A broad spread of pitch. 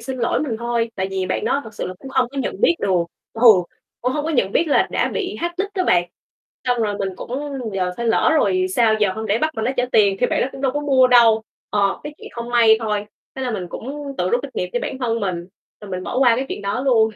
No: average, 4.4 semitones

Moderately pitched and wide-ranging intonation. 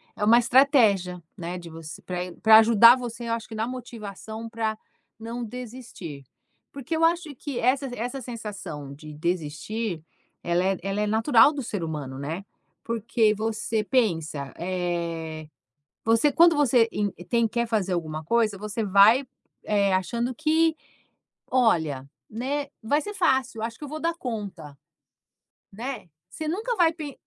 No: high, 225 Hz; wide, 5.8 semitones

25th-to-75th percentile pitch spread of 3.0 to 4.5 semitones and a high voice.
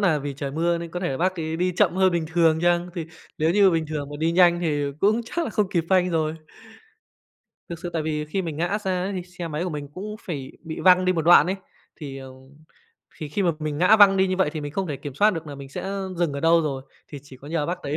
No: average, 3.3 semitones; medium, 170 Hz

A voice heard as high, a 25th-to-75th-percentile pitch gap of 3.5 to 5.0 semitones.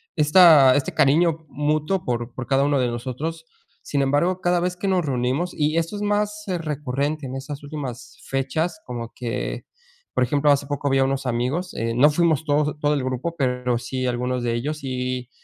No: medium, 140 Hz; average, 3.9 semitones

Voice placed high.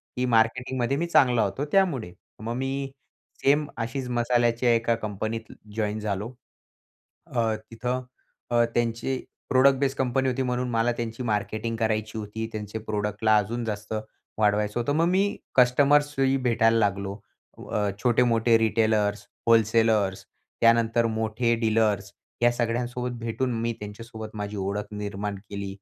No: low, 115 Hz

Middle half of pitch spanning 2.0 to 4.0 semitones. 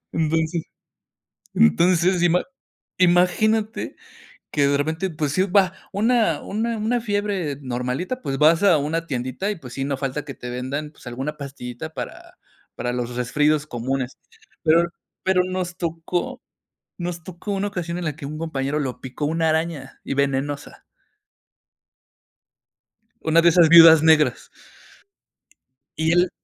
No: average, 4.4 semitones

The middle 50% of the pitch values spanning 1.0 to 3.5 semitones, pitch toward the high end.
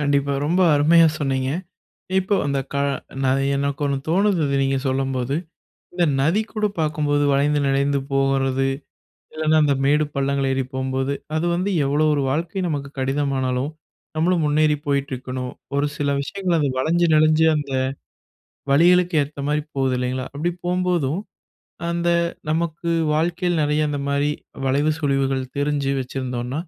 No: average, 2.8 semitones; medium, 145 Hz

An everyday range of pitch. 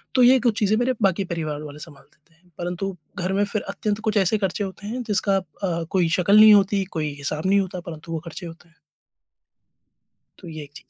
Yes: average, 3.7 semitones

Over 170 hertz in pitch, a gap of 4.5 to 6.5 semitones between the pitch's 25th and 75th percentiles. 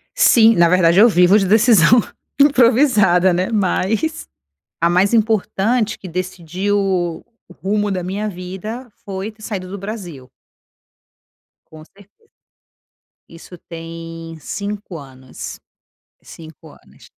No: high, 190 Hz; average, 3.8 semitones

